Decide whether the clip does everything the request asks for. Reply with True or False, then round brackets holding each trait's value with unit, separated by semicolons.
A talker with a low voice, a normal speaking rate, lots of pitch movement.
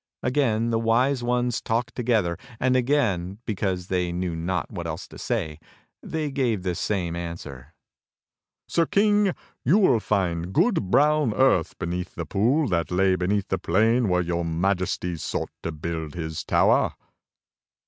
True (95 Hz; 150 wpm; 6.1 semitones)